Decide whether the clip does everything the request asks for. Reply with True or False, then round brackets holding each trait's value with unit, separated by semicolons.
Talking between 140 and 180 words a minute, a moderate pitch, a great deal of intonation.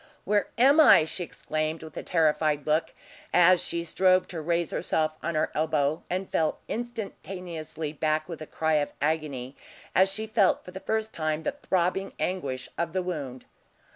False (170 wpm; 165 Hz; 3.2 semitones)